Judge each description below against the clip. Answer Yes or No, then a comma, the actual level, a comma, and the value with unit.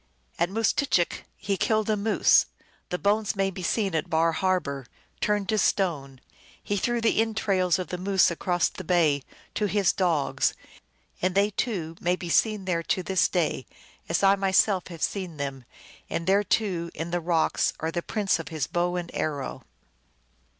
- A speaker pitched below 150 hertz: No, medium, 185 Hz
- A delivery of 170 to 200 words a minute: Yes, average, 180 wpm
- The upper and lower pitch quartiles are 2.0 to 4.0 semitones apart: Yes, average, 3.2 semitones